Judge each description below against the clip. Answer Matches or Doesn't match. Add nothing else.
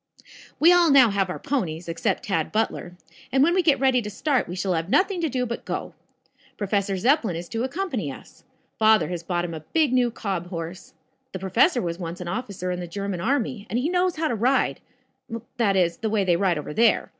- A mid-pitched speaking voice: Doesn't match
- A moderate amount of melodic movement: Doesn't match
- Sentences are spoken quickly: Matches